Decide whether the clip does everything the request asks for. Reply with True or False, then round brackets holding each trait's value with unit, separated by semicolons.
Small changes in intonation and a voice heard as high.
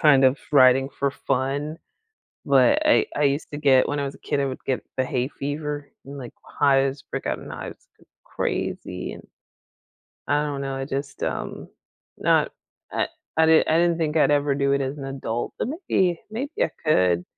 False (1.9 semitones; 140 Hz)